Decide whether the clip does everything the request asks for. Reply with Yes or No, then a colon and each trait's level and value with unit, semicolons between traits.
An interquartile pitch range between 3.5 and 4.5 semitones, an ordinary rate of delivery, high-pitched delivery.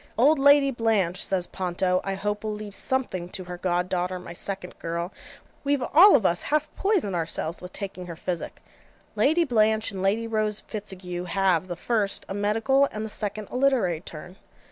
Yes: average, 4.2 semitones; average, 185 wpm; high, 200 Hz